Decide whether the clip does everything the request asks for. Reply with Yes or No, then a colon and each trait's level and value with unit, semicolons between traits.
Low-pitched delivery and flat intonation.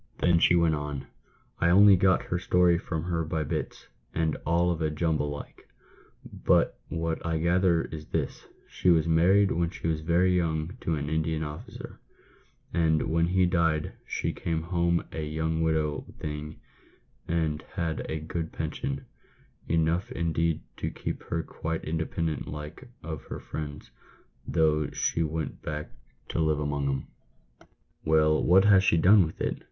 Yes: very low, 80 Hz; narrow, 1.8 semitones